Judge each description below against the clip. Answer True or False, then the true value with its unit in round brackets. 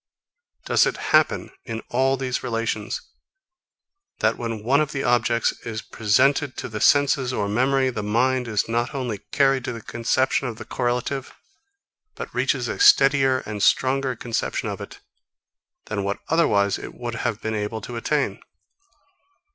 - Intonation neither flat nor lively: True (3.1 semitones)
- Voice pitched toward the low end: True (120 Hz)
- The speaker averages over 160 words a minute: False (155 wpm)